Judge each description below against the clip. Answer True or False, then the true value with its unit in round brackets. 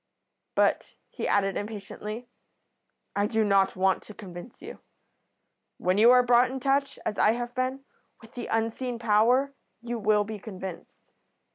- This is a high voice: True (225 Hz)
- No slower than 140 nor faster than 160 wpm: True (150 wpm)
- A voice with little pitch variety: False (3.2 semitones)